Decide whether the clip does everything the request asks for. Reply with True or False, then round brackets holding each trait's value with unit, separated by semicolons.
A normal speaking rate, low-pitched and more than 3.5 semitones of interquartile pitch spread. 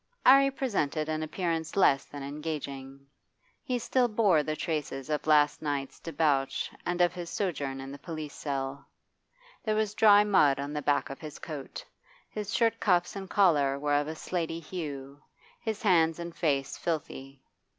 False (165 wpm; 155 Hz; 4.4 semitones)